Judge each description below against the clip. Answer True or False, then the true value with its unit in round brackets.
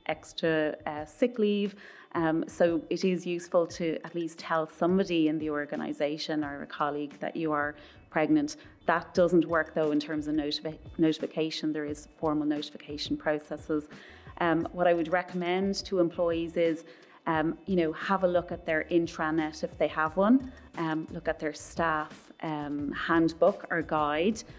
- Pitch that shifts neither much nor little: False (2.1 semitones)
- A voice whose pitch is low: False (160 Hz)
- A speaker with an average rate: True (165 wpm)